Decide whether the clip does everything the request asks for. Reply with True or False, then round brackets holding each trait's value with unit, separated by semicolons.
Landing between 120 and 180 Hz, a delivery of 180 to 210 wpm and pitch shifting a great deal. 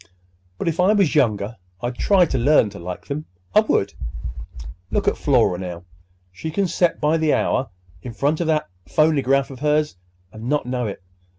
True (140 Hz; 185 wpm; 6.3 semitones)